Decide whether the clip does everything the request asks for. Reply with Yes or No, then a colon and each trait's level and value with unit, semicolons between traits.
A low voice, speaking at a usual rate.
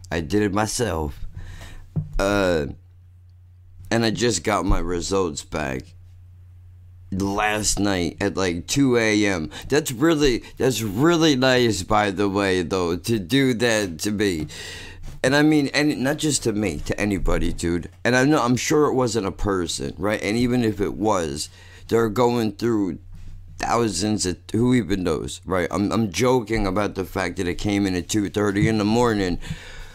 Yes: low, 100 Hz; average, 165 wpm